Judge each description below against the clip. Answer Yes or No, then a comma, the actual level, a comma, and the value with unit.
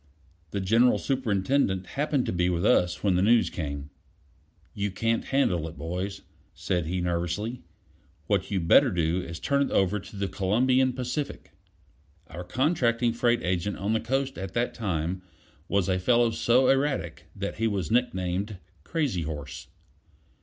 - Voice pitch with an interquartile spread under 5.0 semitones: No, wide, 5.4 semitones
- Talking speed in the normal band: Yes, average, 160 wpm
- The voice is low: Yes, low, 100 Hz